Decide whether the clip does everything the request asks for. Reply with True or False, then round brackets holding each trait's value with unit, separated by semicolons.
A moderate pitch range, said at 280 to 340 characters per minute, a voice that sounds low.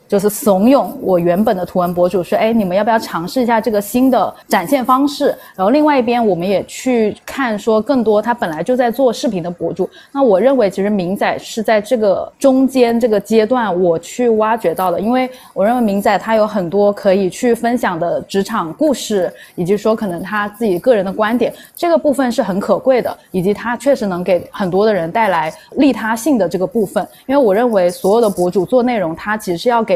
False (4.7 semitones; 325 characters per minute; 220 Hz)